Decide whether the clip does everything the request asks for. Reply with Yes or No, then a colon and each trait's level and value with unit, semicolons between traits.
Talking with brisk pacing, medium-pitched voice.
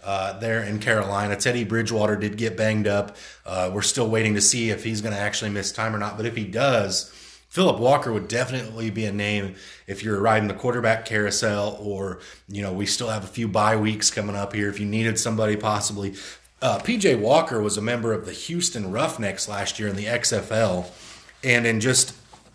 No: fast, 210 wpm; low, 110 Hz